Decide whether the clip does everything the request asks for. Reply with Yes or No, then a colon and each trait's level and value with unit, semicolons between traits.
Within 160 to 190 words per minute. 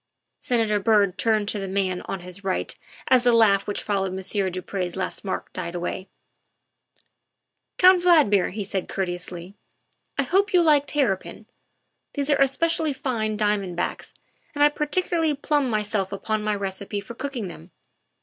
Yes: average, 165 wpm